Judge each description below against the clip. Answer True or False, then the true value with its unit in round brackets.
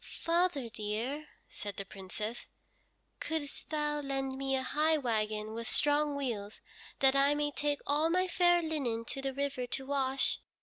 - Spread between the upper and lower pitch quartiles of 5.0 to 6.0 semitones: False (4.2 semitones)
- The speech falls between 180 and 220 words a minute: False (160 wpm)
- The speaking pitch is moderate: False (275 Hz)